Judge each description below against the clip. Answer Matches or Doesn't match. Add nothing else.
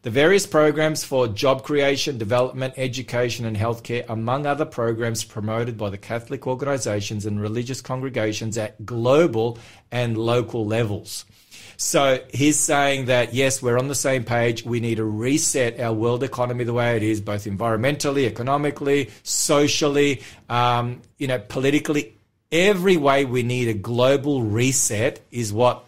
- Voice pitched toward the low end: Matches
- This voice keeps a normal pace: Matches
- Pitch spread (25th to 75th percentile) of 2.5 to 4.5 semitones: Matches